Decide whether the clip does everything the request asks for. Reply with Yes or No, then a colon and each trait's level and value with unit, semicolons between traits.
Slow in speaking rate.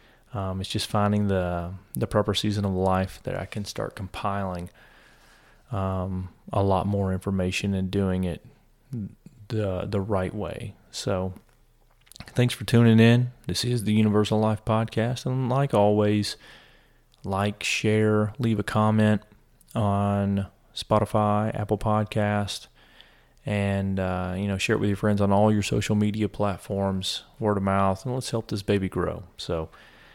No: average, 150 wpm